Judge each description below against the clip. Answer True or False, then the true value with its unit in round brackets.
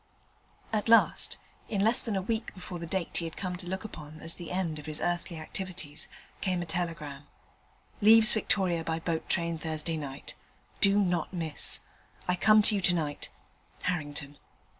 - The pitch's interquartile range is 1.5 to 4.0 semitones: True (3.2 semitones)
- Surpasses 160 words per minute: True (175 wpm)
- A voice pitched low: False (175 Hz)